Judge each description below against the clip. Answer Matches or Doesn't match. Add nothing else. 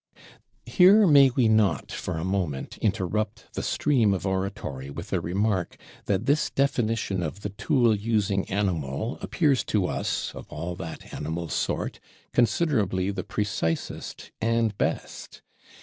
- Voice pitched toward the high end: Doesn't match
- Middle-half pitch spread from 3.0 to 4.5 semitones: Matches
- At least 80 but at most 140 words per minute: Matches